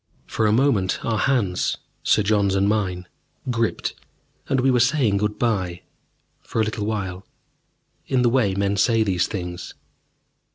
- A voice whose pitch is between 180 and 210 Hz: No, low, 105 Hz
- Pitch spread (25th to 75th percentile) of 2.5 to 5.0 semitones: Yes, average, 3.4 semitones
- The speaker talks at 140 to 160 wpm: Yes, average, 155 wpm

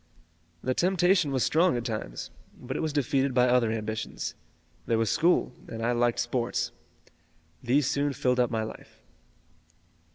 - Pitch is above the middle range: No, low, 125 Hz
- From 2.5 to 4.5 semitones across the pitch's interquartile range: Yes, average, 3.7 semitones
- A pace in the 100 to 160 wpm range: Yes, average, 155 wpm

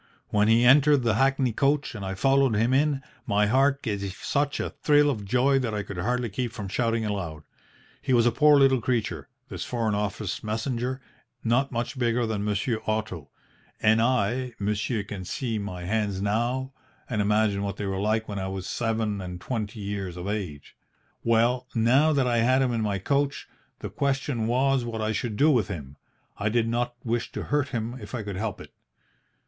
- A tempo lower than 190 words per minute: No, average, 195 wpm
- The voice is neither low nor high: No, low, 115 Hz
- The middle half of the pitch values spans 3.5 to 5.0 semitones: Yes, average, 3.8 semitones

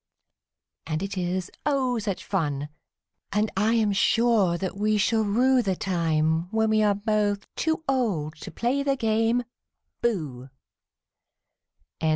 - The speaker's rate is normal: No, slow, 130 wpm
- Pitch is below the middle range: No, high, 210 Hz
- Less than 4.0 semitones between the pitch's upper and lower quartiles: No, average, 4.4 semitones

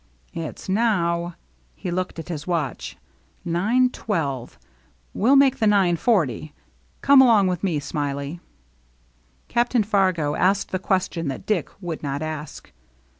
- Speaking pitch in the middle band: Yes, medium, 175 Hz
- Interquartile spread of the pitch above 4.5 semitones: Yes, average, 5.3 semitones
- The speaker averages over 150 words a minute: No, average, 145 wpm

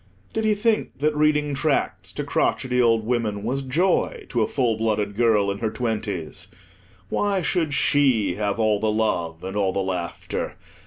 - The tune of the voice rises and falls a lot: Yes, wide, 5.8 semitones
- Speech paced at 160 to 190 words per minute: Yes, average, 170 wpm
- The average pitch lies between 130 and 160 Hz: No, low, 115 Hz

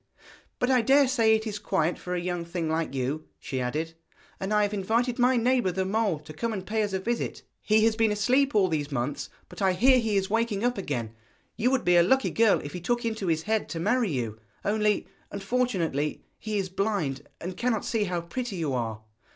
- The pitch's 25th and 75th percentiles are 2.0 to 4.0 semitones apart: No, wide, 5.6 semitones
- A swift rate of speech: Yes, fast, 225 wpm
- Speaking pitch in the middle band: No, high, 200 Hz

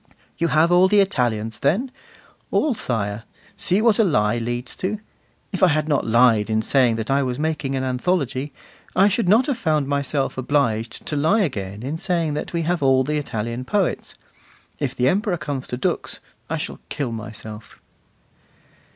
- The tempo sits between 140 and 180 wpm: Yes, average, 175 wpm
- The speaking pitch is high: No, medium, 140 Hz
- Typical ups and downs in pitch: No, wide, 6.8 semitones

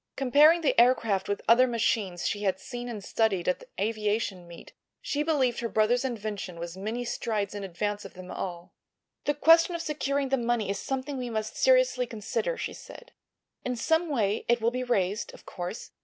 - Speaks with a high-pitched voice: Yes, high, 230 Hz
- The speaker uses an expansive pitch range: No, average, 4.6 semitones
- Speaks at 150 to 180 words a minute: No, average, 190 wpm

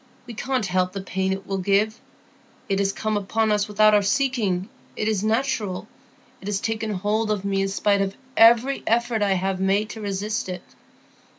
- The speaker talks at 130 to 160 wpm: No, average, 190 wpm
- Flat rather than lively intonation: Yes, narrow, 2.2 semitones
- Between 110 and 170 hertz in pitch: No, high, 205 Hz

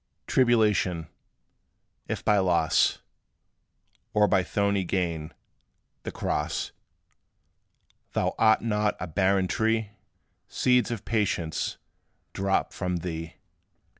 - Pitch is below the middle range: Yes, very low, 95 Hz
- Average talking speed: No, slow, 95 wpm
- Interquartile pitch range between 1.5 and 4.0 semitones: Yes, average, 3.5 semitones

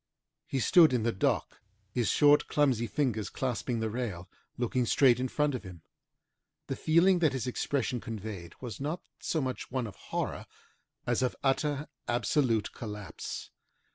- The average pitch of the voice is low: Yes, low, 125 Hz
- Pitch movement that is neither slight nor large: Yes, average, 4.2 semitones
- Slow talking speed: No, average, 155 wpm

